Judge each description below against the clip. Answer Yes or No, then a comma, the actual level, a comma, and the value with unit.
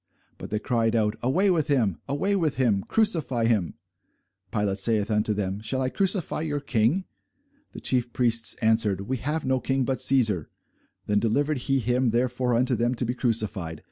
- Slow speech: No, average, 175 wpm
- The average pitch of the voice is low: Yes, low, 120 Hz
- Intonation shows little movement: No, average, 3.9 semitones